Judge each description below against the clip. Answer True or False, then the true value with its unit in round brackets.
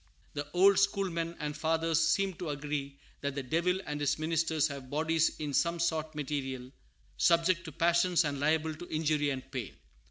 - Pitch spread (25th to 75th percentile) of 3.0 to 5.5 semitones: False (2.6 semitones)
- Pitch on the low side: False (155 Hz)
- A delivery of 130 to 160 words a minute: False (170 wpm)